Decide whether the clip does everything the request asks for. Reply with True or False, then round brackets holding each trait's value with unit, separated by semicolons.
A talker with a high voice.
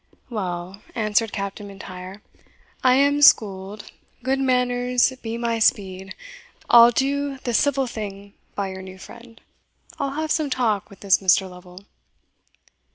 True (220 Hz)